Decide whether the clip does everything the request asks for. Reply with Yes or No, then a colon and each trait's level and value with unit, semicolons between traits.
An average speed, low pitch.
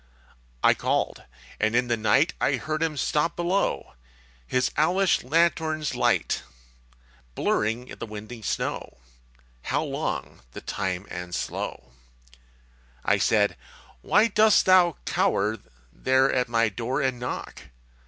No: slow, 125 wpm; low, 130 Hz